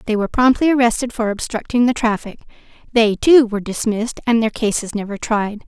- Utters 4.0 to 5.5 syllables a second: No, 5.9 syllables/s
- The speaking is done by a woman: Yes, female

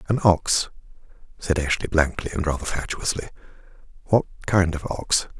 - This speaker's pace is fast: No, slow, 135 wpm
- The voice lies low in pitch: Yes, very low, 85 Hz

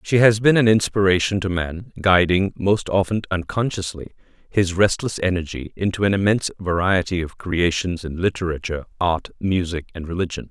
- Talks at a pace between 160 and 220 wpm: No, average, 150 wpm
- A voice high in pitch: No, very low, 95 Hz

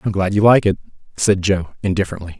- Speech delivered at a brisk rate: Yes, fast, 225 wpm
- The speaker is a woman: No, male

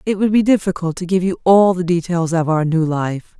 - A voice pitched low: No, medium, 175 Hz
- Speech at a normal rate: No, fast, 250 wpm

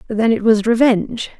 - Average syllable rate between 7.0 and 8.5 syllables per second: No, 5.2 syllables/s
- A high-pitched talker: Yes, high, 225 Hz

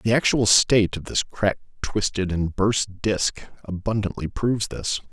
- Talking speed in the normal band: Yes, average, 150 wpm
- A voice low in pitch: Yes, low, 105 Hz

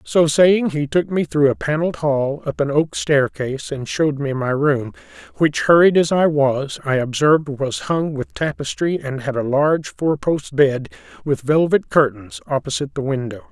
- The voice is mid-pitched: Yes, medium, 145 Hz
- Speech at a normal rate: Yes, average, 180 wpm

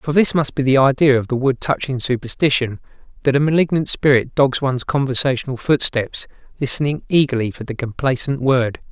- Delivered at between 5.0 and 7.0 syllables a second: Yes, 5.6 syllables/s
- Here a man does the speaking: Yes, male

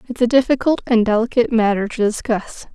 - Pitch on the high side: Yes, high, 230 Hz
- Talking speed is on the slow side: No, average, 175 wpm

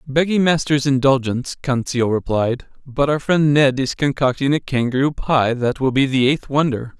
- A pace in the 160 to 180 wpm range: Yes, average, 170 wpm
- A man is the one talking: Yes, male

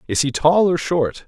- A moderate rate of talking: No, fast, 235 wpm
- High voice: No, medium, 155 Hz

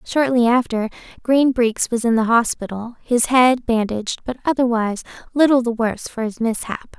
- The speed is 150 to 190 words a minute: Yes, average, 165 wpm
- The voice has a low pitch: No, high, 235 Hz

